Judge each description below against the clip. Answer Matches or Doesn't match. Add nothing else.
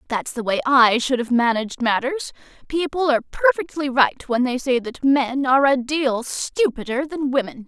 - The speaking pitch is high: Matches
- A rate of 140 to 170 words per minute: Doesn't match